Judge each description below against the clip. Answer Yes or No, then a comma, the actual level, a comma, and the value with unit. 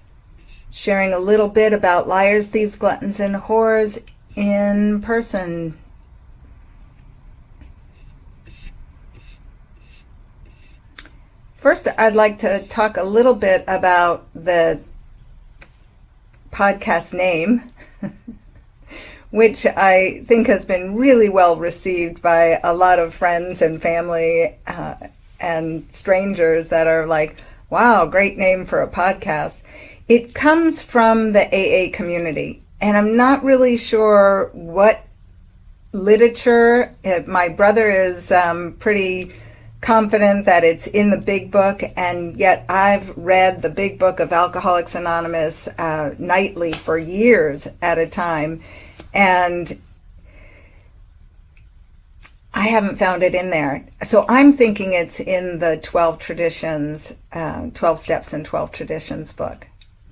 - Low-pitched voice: No, medium, 180 Hz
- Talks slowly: Yes, slow, 115 wpm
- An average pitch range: Yes, average, 4.0 semitones